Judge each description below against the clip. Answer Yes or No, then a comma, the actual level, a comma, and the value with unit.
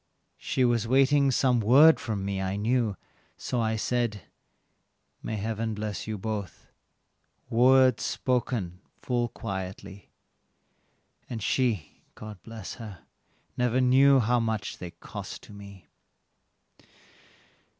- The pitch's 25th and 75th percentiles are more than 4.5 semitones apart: No, average, 3.6 semitones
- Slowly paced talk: Yes, slow, 115 wpm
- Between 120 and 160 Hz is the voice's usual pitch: No, low, 110 Hz